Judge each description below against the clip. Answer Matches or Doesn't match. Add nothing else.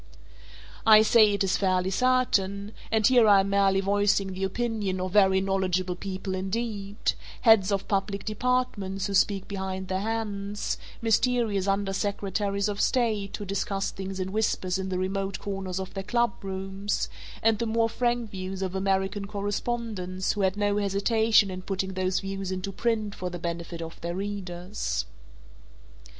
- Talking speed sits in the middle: Matches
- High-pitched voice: Matches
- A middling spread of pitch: Doesn't match